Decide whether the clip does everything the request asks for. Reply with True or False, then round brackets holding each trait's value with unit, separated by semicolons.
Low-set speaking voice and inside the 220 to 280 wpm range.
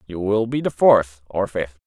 True (100 Hz; 225 wpm)